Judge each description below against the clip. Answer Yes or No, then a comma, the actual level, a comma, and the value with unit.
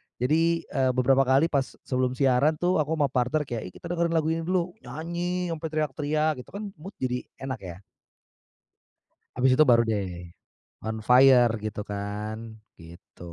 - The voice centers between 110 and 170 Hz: Yes, low, 135 Hz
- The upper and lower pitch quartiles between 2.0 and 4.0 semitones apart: No, average, 4.8 semitones